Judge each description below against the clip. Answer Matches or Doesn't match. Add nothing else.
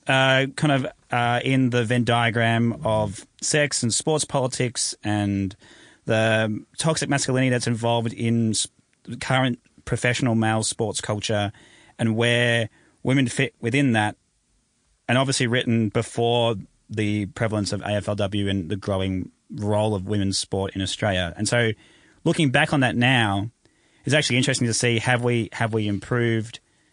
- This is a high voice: Doesn't match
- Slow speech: Doesn't match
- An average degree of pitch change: Matches